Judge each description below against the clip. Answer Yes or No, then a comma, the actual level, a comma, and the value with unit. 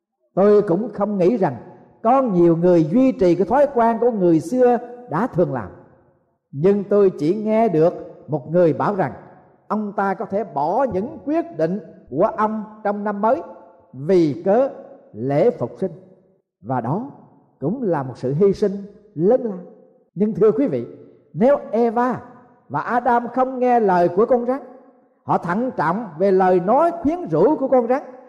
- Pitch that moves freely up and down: Yes, wide, 5.7 semitones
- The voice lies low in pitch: No, high, 205 Hz